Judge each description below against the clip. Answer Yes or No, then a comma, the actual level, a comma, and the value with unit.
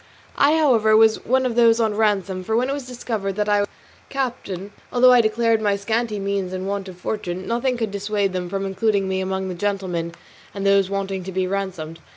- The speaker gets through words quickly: Yes, fast, 215 wpm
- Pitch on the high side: Yes, high, 200 Hz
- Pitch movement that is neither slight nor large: Yes, average, 3.0 semitones